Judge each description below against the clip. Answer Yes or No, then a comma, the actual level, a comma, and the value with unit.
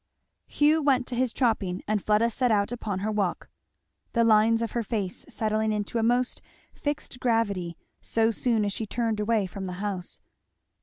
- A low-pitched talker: No, high, 220 Hz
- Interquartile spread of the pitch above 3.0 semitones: No, narrow, 2.6 semitones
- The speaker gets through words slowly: No, average, 175 wpm